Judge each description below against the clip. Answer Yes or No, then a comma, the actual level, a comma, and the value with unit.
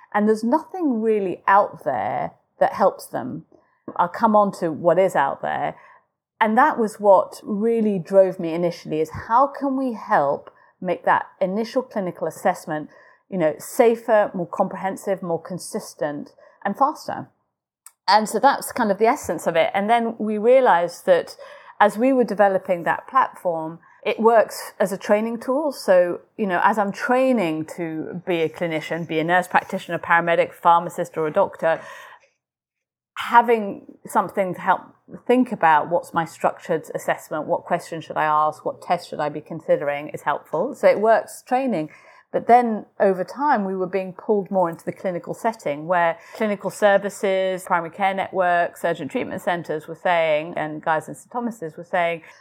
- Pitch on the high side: Yes, high, 195 Hz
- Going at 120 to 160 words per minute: No, average, 170 wpm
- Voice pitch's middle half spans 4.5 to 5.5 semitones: Yes, average, 5.0 semitones